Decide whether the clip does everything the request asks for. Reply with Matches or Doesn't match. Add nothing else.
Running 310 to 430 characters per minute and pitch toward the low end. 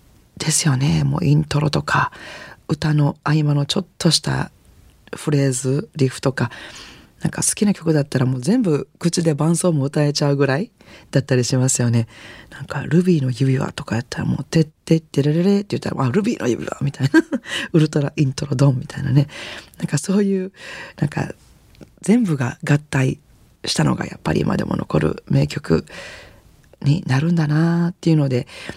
Doesn't match